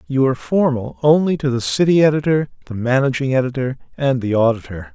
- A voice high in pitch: No, low, 130 Hz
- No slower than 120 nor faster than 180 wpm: Yes, average, 170 wpm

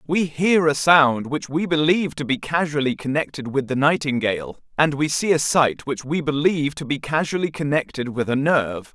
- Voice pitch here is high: No, medium, 145 Hz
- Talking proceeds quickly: No, average, 195 wpm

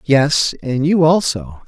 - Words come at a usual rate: Yes, average, 145 wpm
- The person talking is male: Yes, male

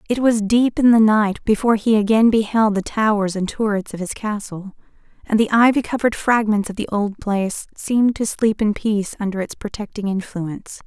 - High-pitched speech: Yes, high, 215 Hz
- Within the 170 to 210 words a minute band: Yes, average, 195 wpm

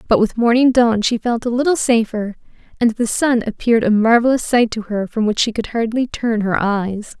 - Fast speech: Yes, fast, 215 wpm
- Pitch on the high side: Yes, high, 225 Hz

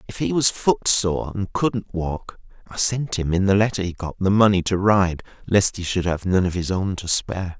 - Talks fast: Yes, fast, 230 wpm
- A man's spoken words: Yes, male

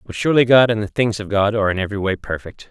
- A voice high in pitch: No, low, 105 Hz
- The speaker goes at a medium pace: No, fast, 290 wpm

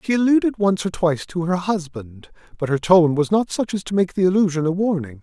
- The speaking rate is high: Yes, fast, 240 wpm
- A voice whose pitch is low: No, medium, 180 Hz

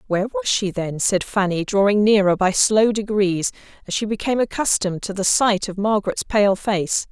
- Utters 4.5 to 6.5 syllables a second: Yes, 5.2 syllables/s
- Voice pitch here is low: No, high, 205 Hz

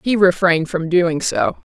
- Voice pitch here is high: No, medium, 180 Hz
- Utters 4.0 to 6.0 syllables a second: Yes, 4.5 syllables/s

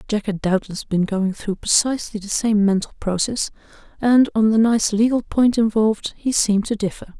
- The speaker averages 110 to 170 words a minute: No, average, 185 wpm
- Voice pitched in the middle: No, high, 215 Hz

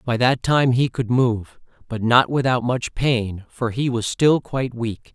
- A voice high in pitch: No, low, 120 Hz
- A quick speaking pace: Yes, fast, 210 wpm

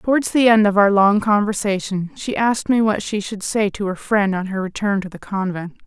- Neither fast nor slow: No, fast, 235 wpm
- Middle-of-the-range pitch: No, high, 205 Hz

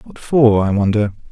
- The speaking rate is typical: Yes, average, 180 wpm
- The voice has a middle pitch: No, low, 115 Hz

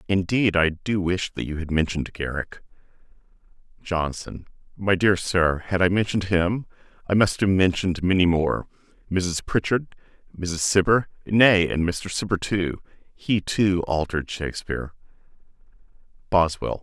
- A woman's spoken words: No, male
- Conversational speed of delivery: No, slow, 130 wpm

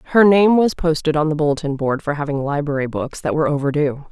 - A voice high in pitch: No, medium, 150 Hz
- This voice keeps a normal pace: No, fast, 220 wpm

